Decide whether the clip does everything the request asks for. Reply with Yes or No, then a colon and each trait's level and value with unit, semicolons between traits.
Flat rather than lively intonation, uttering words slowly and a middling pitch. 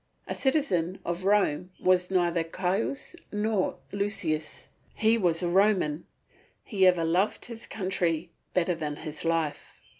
No: average, 3.4 semitones; slow, 130 wpm; medium, 180 Hz